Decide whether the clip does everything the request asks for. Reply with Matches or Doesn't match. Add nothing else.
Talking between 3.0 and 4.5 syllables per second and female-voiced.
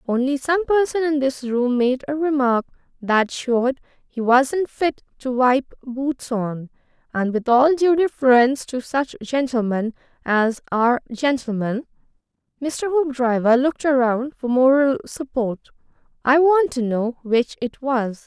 Matches